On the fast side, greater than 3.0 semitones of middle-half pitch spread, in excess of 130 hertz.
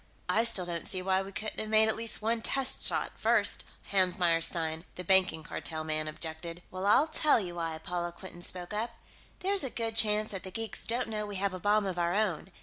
Yes: fast, 225 wpm; average, 4.1 semitones; high, 190 Hz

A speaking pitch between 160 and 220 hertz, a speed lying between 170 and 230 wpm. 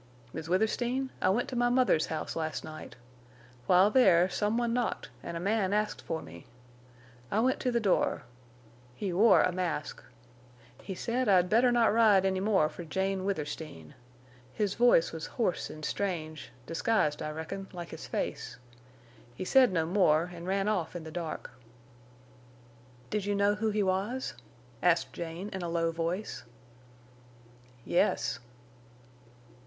No: high, 190 Hz; average, 155 wpm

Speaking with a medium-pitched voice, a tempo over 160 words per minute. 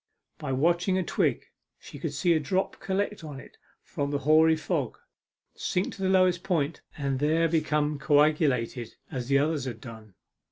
Yes: medium, 150 Hz; average, 170 wpm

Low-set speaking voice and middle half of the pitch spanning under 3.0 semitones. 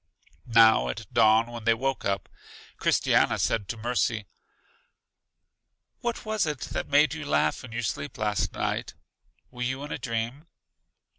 No: low, 115 Hz; average, 3.8 semitones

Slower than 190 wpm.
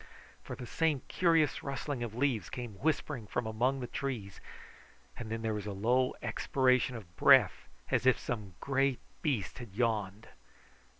Yes: average, 160 wpm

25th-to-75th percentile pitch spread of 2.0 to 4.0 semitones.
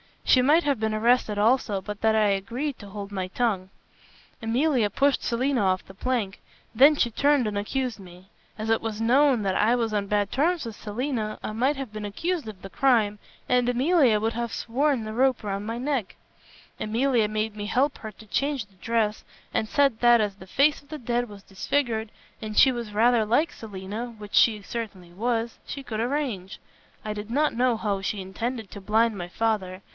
Yes: average, 3.5 semitones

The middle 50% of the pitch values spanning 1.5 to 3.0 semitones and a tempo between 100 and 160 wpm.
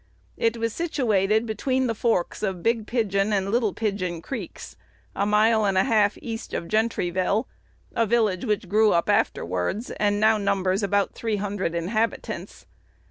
Yes: average, 2.7 semitones; average, 155 wpm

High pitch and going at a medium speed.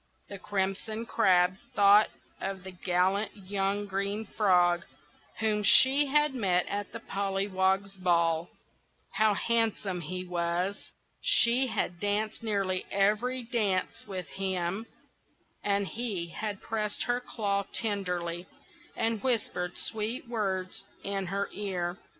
No: high, 200 Hz; slow, 120 wpm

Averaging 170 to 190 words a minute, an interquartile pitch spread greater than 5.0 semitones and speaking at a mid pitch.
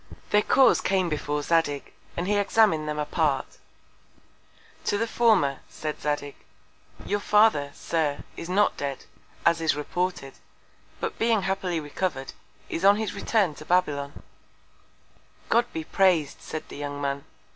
No: average, 140 wpm; wide, 5.5 semitones; medium, 165 Hz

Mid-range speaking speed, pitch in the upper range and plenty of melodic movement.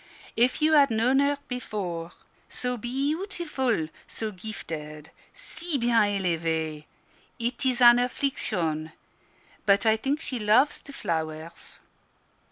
No: slow, 120 wpm; high, 225 Hz; wide, 8.0 semitones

